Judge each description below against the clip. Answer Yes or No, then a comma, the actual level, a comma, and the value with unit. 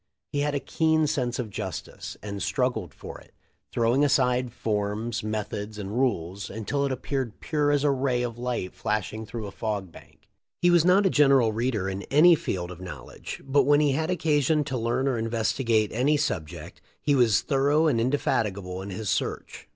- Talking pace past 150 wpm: Yes, average, 190 wpm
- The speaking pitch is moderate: No, low, 120 Hz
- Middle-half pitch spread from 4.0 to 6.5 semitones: Yes, average, 5.2 semitones